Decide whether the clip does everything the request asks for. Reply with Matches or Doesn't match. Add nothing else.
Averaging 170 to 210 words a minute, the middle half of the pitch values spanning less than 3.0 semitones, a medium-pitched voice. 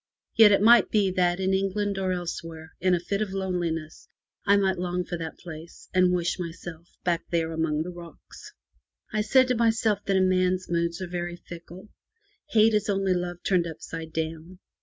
Matches